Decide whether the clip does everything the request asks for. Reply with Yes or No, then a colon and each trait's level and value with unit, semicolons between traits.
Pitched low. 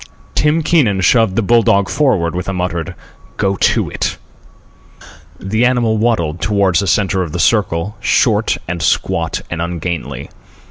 Yes: very low, 95 Hz